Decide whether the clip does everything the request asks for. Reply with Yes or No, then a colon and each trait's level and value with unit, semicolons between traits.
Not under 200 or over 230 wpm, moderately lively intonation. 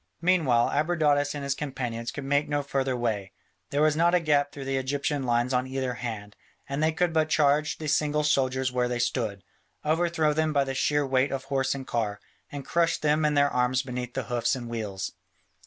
Yes: fast, 205 wpm; average, 3.3 semitones